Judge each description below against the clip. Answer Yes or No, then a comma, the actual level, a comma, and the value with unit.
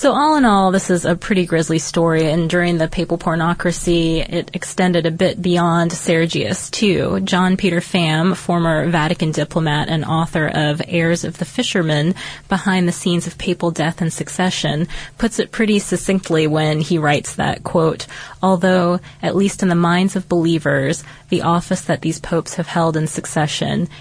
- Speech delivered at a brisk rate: No, average, 170 wpm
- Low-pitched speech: No, medium, 170 Hz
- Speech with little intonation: Yes, narrow, 2.2 semitones